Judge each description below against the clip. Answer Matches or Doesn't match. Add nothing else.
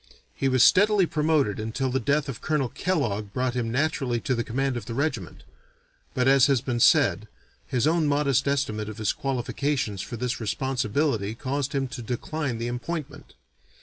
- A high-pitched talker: Doesn't match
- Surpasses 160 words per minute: Matches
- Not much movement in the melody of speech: Doesn't match